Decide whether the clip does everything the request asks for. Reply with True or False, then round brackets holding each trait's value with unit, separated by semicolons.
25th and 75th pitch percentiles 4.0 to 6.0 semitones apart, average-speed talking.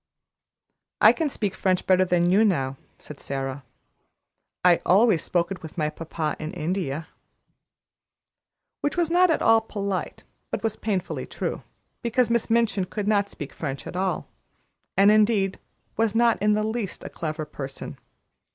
True (5.2 semitones; 155 wpm)